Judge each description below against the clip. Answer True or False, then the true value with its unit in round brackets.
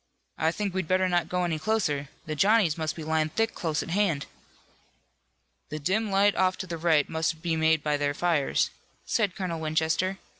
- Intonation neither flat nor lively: True (3.1 semitones)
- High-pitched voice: False (165 Hz)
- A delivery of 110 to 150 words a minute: False (190 wpm)